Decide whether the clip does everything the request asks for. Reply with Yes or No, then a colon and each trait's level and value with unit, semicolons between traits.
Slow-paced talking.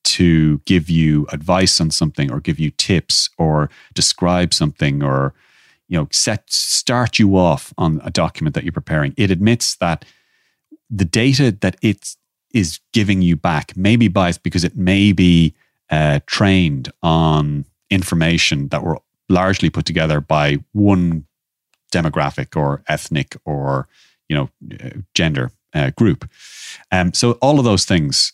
No: average, 150 wpm